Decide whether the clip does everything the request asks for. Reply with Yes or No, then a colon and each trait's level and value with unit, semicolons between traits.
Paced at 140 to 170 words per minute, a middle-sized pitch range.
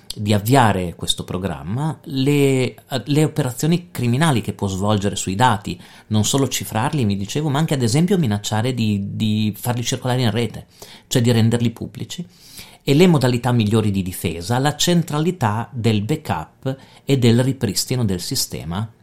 Yes: average, 150 wpm; average, 4.9 semitones